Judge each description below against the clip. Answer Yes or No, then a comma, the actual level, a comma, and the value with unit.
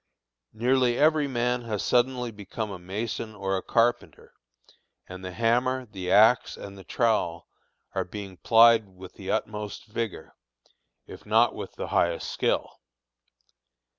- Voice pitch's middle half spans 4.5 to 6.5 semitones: No, average, 3.9 semitones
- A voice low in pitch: Yes, low, 110 Hz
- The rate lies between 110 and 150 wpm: Yes, slow, 135 wpm